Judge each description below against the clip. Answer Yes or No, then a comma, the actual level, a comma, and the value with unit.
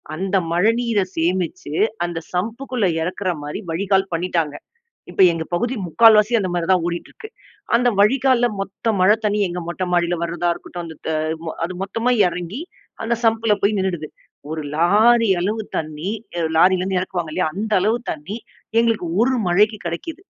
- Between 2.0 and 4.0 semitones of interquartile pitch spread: No, average, 4.4 semitones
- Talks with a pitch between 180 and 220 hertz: Yes, high, 190 Hz